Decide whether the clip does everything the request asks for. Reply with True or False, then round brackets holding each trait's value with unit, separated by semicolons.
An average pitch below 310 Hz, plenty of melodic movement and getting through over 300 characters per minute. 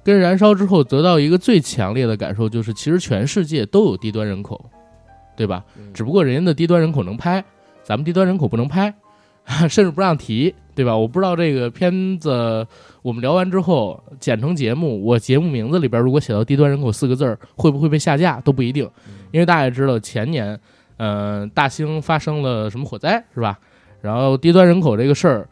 True (135 Hz; 7.4 semitones; 320 characters per minute)